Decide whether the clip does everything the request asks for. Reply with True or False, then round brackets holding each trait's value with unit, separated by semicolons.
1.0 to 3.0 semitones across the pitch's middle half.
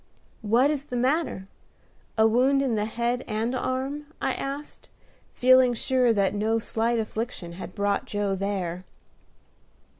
False (3.9 semitones)